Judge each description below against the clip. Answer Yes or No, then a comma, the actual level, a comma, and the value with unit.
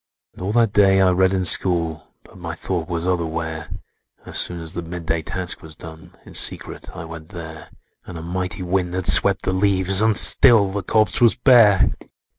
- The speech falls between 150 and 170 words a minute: No, average, 195 wpm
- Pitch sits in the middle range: No, very low, 90 Hz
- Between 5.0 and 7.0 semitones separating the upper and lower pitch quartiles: No, average, 2.8 semitones